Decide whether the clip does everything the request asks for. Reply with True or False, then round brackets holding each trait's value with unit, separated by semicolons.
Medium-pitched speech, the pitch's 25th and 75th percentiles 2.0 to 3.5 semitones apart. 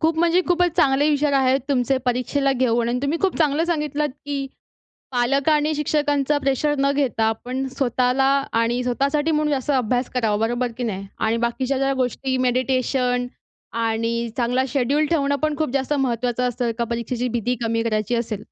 False (260 Hz; 3.2 semitones)